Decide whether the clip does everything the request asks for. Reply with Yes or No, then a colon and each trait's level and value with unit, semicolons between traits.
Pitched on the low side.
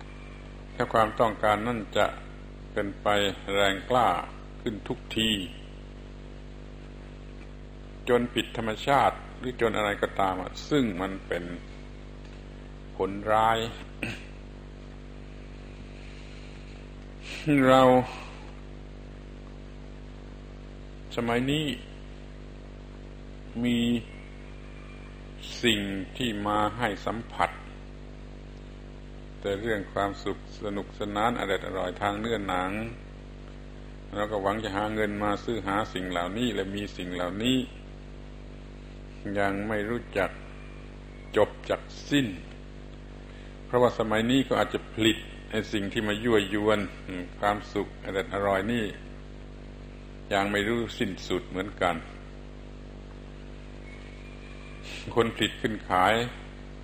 Yes: low, 105 Hz